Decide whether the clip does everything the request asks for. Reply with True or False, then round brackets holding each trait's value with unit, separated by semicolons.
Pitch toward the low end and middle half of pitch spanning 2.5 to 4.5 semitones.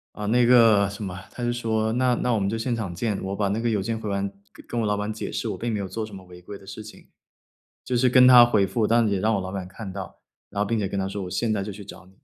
True (105 Hz; 2.9 semitones)